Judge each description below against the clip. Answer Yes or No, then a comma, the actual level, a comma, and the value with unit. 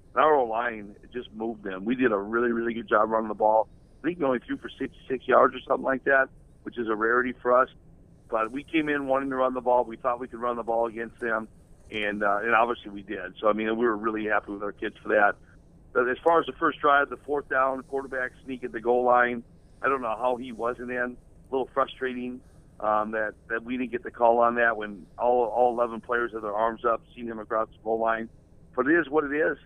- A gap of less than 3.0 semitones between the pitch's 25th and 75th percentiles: Yes, narrow, 2.5 semitones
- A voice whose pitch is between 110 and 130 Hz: Yes, low, 120 Hz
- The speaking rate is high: Yes, fast, 255 wpm